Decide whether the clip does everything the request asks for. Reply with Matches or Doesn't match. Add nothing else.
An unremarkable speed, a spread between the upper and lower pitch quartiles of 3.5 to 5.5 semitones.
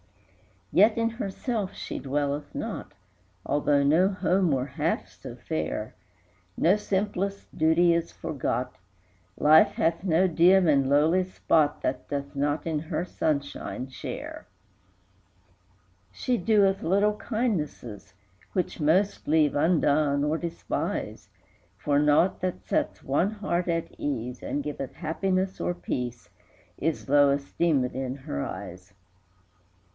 Doesn't match